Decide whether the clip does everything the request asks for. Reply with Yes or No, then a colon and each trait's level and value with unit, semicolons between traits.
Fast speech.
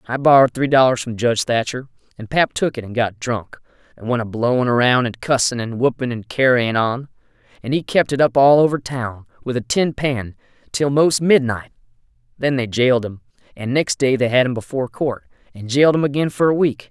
Yes: fast, 215 wpm